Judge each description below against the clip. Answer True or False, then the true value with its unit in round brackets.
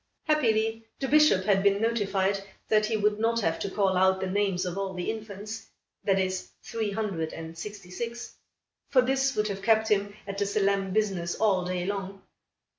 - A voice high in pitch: True (200 Hz)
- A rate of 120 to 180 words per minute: False (190 wpm)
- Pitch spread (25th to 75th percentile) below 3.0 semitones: True (2.6 semitones)